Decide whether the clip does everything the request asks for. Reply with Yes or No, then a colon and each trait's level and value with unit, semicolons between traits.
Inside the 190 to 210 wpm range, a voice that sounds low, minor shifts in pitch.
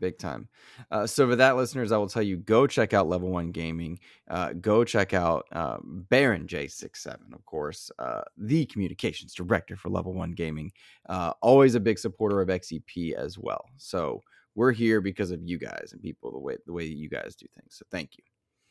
No: fast, 205 wpm; low, 100 Hz; average, 4.8 semitones